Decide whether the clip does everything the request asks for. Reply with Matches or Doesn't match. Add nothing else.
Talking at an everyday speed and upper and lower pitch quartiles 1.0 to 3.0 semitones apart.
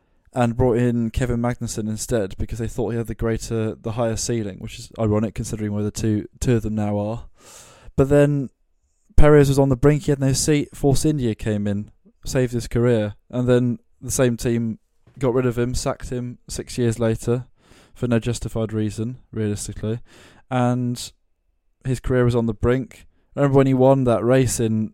Matches